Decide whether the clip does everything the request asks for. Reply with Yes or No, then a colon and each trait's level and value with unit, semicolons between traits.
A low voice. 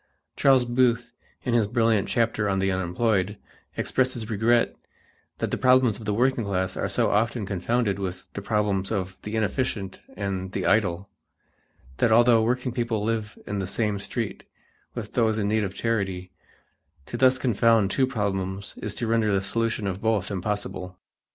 Yes: low, 105 Hz